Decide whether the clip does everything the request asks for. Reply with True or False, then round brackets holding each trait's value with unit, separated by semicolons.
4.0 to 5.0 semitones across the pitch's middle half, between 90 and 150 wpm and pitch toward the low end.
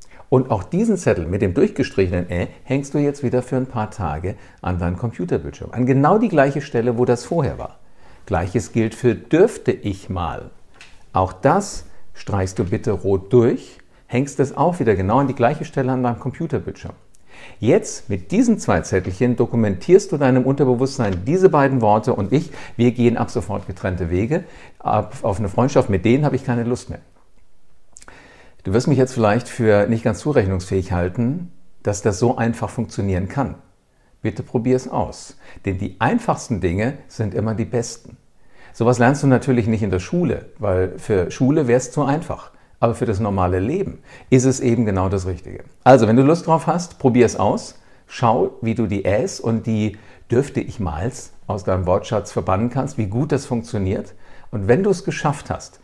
False (4.7 semitones; 185 wpm; 120 Hz)